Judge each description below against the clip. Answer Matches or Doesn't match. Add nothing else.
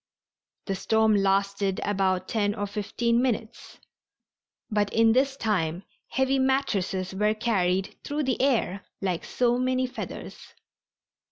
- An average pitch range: Matches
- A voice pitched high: Matches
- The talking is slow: Matches